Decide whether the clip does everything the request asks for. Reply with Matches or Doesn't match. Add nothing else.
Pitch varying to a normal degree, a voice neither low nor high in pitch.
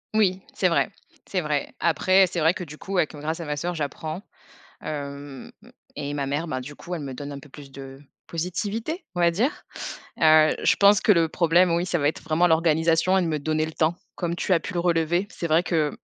Matches